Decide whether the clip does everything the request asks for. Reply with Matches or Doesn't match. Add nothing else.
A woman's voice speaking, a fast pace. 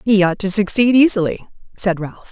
Doesn't match